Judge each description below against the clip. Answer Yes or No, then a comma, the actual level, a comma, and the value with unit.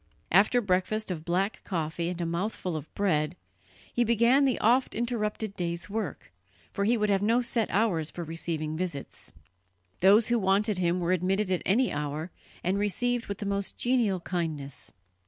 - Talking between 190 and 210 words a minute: No, average, 170 wpm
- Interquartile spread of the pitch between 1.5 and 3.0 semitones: No, average, 4.2 semitones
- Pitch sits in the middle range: No, high, 195 Hz